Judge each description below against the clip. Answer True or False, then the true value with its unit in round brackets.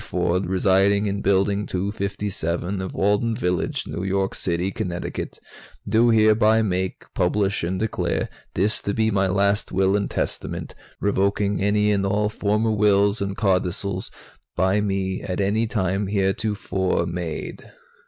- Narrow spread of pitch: True (1.7 semitones)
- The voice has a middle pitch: False (100 Hz)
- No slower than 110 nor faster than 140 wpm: True (135 wpm)